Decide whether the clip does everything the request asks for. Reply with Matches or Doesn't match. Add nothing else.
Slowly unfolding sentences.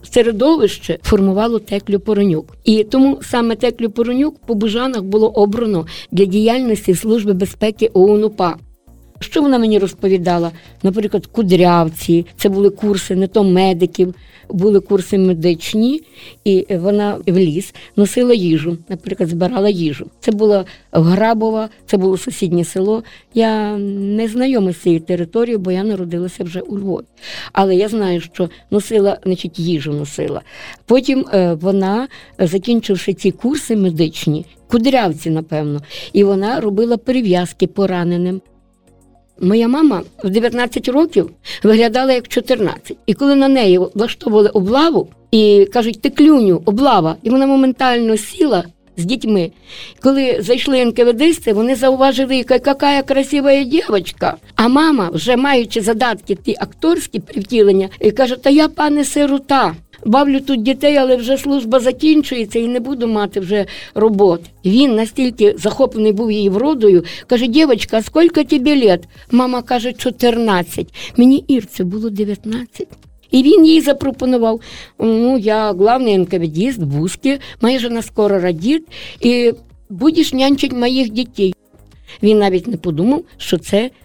Doesn't match